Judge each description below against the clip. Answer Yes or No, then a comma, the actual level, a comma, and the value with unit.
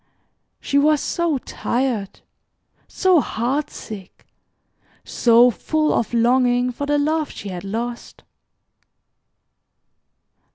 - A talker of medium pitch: No, very high, 250 Hz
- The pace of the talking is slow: Yes, slow, 95 wpm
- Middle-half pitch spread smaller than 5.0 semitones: Yes, average, 4.1 semitones